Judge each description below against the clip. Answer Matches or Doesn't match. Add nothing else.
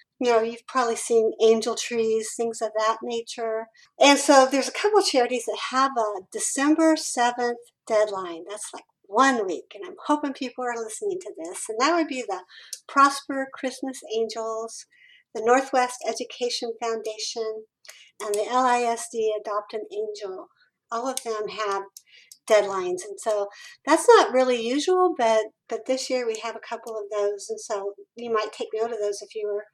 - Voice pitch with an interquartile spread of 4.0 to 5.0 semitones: Doesn't match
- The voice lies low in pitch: Doesn't match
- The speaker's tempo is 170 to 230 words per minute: Matches